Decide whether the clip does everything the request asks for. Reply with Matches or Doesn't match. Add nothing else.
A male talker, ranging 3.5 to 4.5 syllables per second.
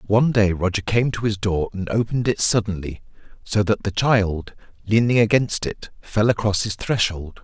Doesn't match